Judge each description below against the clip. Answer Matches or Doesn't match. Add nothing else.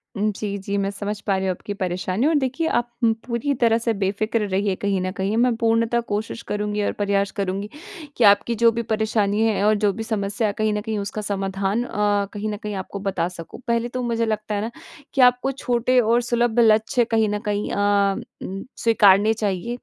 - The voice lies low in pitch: Doesn't match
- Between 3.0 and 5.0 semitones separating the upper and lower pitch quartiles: Doesn't match